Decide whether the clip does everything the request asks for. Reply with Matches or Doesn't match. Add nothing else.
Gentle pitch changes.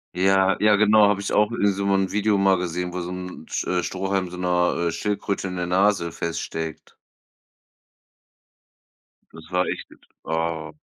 Matches